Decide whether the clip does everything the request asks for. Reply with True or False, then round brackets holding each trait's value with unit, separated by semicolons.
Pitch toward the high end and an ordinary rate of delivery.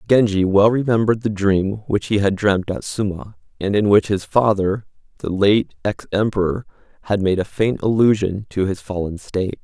False (100 Hz; 180 wpm)